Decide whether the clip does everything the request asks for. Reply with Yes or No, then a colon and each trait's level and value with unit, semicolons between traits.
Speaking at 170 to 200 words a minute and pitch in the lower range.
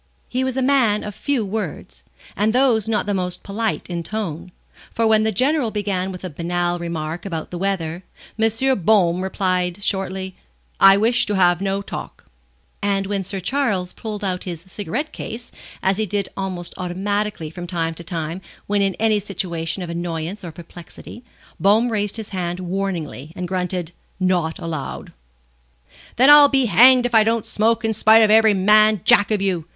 No: average, 175 wpm; high, 195 Hz